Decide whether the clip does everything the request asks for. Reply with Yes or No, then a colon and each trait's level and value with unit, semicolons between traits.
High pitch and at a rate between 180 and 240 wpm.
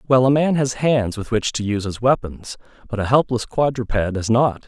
No: low, 120 Hz; fast, 205 wpm